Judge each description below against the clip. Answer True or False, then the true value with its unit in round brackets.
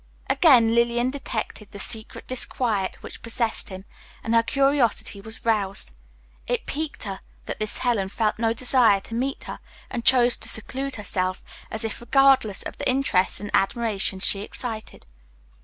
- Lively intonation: False (3.4 semitones)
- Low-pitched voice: False (225 Hz)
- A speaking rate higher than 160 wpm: False (155 wpm)